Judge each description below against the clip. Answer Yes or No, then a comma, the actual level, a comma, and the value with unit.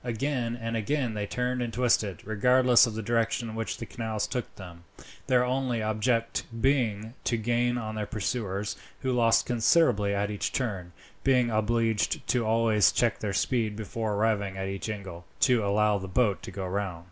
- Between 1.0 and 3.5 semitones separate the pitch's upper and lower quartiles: Yes, average, 2.9 semitones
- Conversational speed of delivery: Yes, average, 180 wpm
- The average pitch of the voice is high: No, low, 110 Hz